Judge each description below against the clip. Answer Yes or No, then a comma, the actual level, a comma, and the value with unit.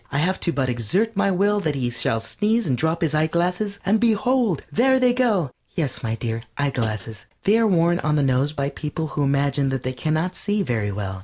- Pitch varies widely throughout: Yes, wide, 7.6 semitones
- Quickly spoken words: Yes, fast, 215 wpm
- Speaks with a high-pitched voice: No, medium, 155 Hz